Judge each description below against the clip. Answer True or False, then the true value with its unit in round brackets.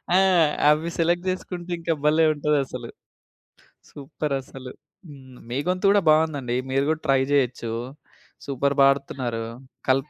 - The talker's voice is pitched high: False (140 Hz)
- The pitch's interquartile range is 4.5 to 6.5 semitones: False (3.5 semitones)